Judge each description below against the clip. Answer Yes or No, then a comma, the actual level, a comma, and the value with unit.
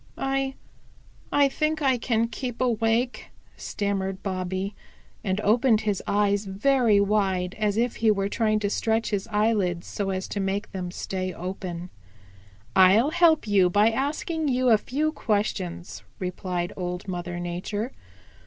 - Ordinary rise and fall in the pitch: Yes, average, 4.0 semitones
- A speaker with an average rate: Yes, average, 145 wpm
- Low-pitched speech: No, high, 205 Hz